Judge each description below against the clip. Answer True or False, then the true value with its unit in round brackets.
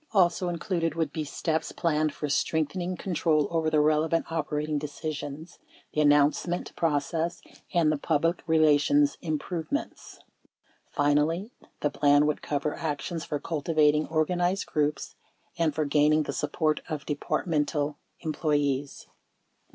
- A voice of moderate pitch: True (155 Hz)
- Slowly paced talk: True (120 wpm)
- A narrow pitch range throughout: True (2.1 semitones)